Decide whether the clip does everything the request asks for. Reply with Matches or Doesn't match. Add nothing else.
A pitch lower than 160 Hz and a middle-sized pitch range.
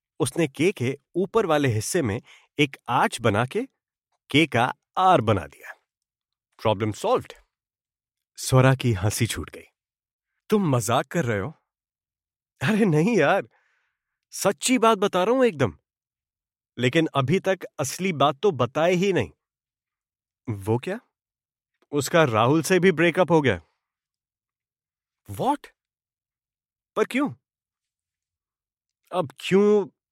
Doesn't match